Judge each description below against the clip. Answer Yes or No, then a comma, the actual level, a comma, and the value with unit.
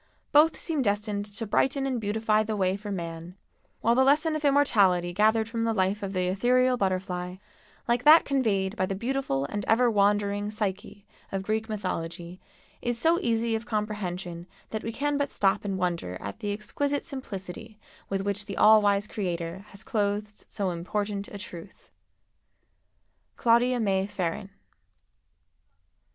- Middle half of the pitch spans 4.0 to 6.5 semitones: No, average, 3.4 semitones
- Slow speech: No, average, 155 wpm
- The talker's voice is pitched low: No, high, 205 Hz